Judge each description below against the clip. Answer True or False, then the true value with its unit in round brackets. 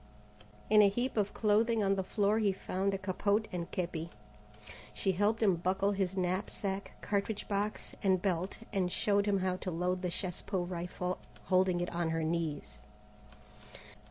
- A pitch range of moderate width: False (2.2 semitones)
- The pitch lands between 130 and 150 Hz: False (190 Hz)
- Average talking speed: True (165 wpm)